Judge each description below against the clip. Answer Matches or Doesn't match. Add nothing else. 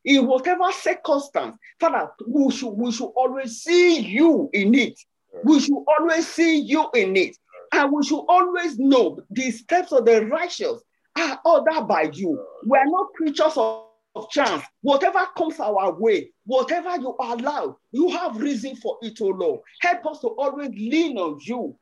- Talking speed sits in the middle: Matches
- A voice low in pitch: Doesn't match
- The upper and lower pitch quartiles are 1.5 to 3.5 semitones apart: Doesn't match